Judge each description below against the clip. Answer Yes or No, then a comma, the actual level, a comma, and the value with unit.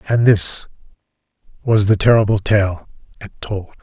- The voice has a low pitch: Yes, low, 105 Hz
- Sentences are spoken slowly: Yes, slow, 125 wpm